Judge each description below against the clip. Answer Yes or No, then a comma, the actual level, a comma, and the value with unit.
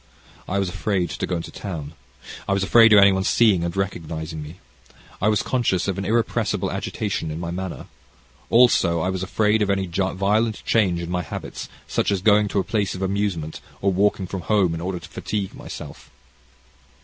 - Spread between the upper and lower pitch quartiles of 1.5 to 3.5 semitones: Yes, average, 2.9 semitones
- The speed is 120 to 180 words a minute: No, average, 195 wpm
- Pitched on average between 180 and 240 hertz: No, very low, 95 Hz